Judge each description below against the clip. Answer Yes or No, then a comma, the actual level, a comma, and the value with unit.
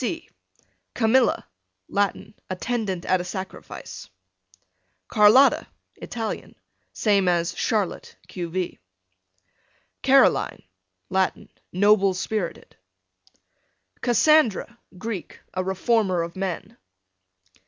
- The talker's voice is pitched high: Yes, high, 195 Hz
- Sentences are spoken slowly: Yes, slow, 80 wpm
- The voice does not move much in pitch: No, average, 3.3 semitones